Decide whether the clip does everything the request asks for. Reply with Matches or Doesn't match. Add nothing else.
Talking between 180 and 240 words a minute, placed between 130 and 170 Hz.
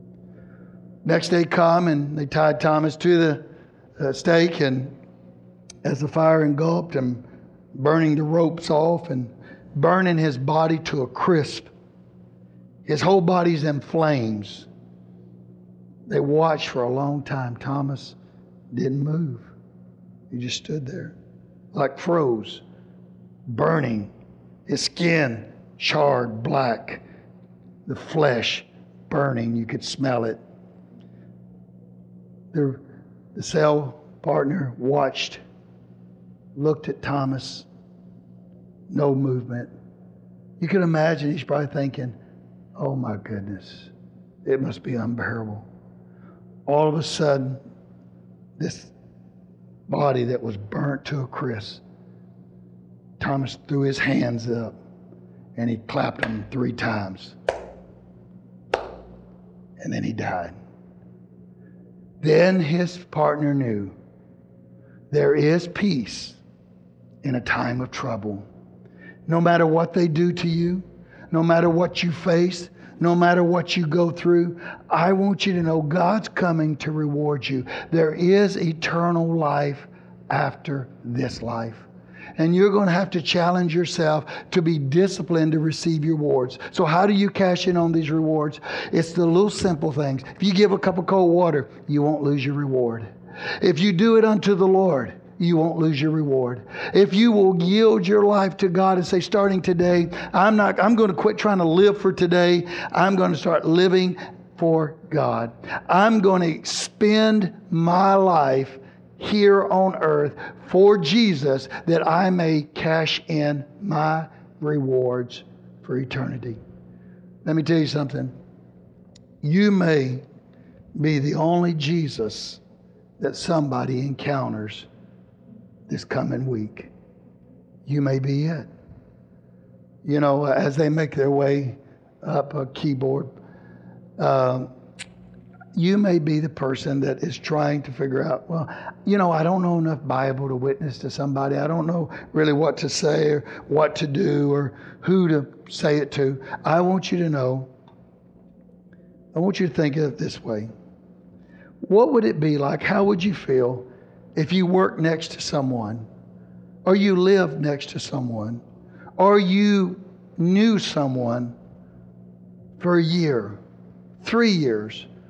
Doesn't match